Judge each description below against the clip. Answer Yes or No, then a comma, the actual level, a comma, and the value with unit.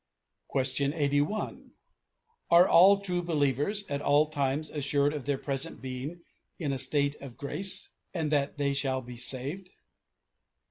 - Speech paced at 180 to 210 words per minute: No, average, 140 wpm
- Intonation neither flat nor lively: Yes, average, 3.4 semitones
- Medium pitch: Yes, medium, 145 Hz